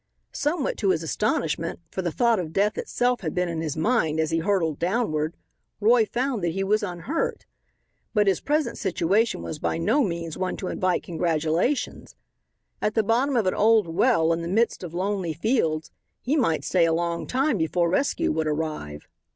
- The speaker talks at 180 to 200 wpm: Yes, average, 185 wpm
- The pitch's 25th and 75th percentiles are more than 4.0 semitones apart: Yes, wide, 5.6 semitones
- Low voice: No, medium, 185 Hz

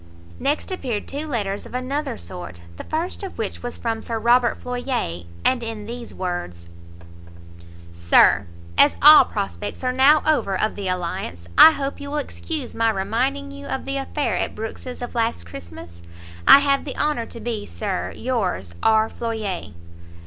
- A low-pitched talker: No, high, 230 Hz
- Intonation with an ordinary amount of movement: No, wide, 6.1 semitones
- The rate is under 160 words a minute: No, average, 165 wpm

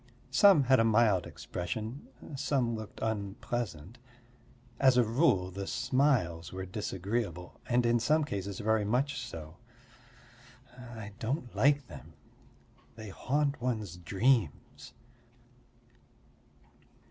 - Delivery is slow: Yes, slow, 105 wpm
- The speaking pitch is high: No, low, 115 Hz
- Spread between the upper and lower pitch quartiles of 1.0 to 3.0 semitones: No, average, 4.7 semitones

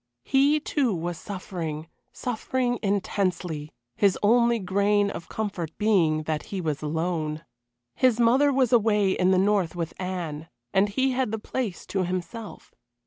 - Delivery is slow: No, average, 145 wpm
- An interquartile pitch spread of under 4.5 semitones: No, average, 5.1 semitones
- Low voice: No, high, 195 Hz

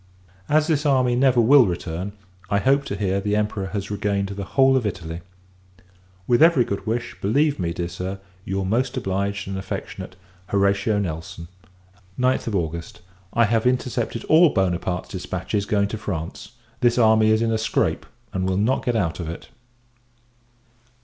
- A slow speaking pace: No, average, 165 wpm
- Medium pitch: No, low, 105 Hz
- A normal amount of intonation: Yes, average, 4.3 semitones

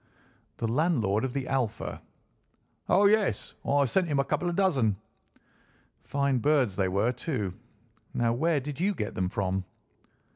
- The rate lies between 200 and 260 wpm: No, average, 150 wpm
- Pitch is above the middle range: No, low, 135 Hz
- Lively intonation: Yes, wide, 6.8 semitones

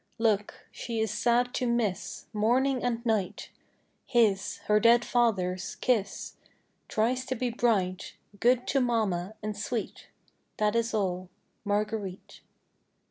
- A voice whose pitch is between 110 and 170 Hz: No, high, 220 Hz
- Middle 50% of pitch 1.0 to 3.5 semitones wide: Yes, average, 2.8 semitones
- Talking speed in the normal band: No, slow, 125 wpm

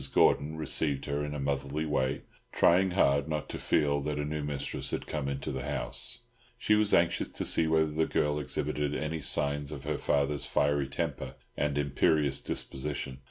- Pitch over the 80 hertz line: No, very low, 75 Hz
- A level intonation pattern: Yes, narrow, 1.7 semitones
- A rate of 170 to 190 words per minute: Yes, average, 180 wpm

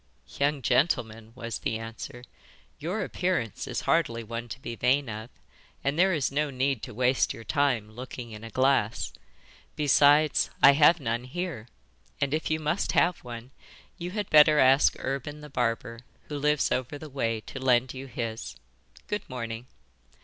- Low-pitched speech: Yes, low, 130 Hz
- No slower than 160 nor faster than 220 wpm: Yes, average, 165 wpm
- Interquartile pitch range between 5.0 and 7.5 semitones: No, average, 4.3 semitones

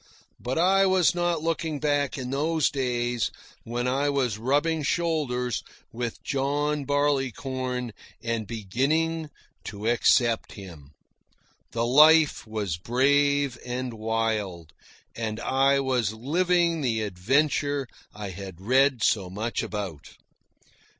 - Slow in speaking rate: Yes, slow, 115 wpm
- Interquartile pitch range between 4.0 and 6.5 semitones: Yes, average, 4.5 semitones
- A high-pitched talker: No, low, 130 Hz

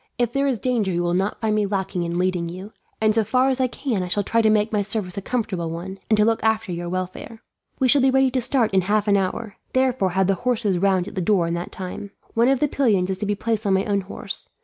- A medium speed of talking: No, fast, 280 wpm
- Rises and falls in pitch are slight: No, average, 3.8 semitones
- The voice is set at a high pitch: Yes, high, 205 Hz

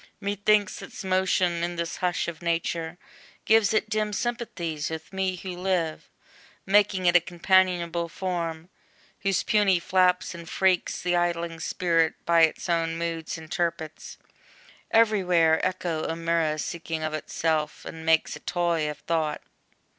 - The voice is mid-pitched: Yes, medium, 170 Hz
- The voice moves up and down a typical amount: No, narrow, 2.3 semitones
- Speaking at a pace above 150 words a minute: No, average, 145 wpm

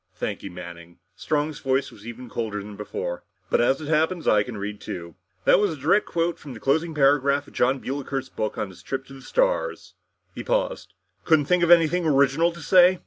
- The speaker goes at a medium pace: No, fast, 215 wpm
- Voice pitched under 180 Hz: Yes, medium, 140 Hz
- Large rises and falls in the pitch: Yes, wide, 6.8 semitones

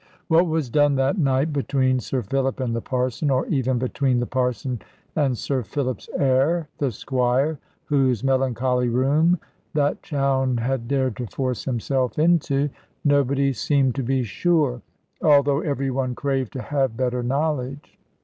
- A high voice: No, low, 135 Hz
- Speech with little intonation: Yes, narrow, 2.1 semitones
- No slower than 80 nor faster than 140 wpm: No, average, 150 wpm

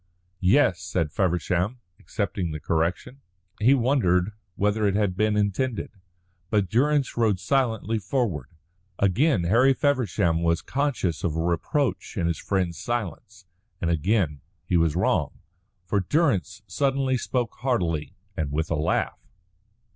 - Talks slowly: Yes, slow, 130 wpm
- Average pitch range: No, wide, 6.3 semitones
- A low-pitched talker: Yes, low, 100 Hz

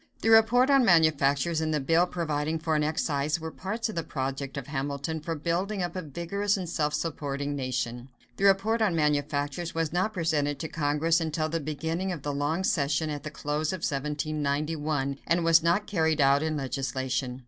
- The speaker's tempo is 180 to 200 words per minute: Yes, average, 190 wpm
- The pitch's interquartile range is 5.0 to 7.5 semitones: No, average, 2.9 semitones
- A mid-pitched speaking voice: Yes, medium, 155 Hz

